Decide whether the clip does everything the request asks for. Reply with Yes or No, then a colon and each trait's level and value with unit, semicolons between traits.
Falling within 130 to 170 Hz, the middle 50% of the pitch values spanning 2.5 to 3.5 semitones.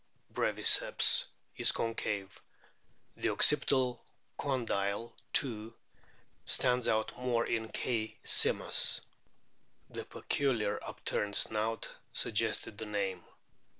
No: low, 110 Hz; average, 2.9 semitones